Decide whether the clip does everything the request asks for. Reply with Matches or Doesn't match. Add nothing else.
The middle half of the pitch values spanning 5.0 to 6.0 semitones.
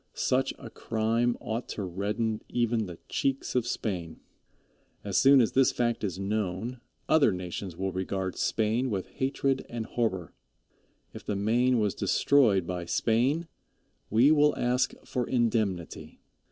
Doesn't match